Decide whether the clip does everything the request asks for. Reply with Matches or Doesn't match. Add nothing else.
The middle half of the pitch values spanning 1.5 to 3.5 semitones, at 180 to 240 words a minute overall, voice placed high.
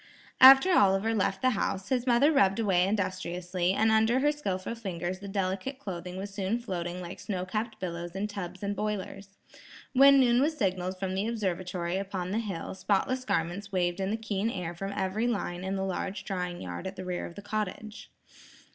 Matches